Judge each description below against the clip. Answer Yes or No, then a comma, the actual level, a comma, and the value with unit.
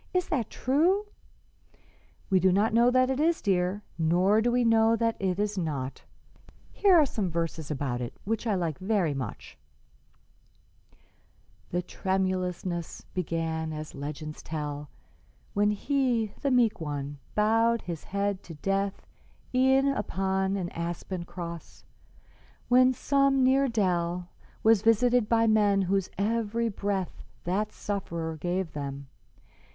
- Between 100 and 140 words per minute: Yes, slow, 135 wpm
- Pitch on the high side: Yes, high, 195 Hz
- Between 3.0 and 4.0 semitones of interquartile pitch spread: No, average, 5.2 semitones